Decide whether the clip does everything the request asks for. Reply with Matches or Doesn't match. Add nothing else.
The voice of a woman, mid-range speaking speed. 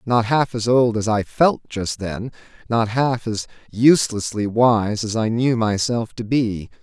Doesn't match